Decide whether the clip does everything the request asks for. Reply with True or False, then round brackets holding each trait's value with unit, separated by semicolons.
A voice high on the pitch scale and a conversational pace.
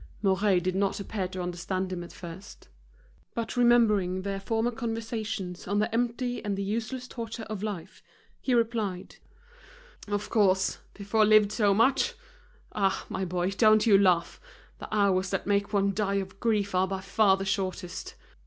True (200 Hz; 160 wpm)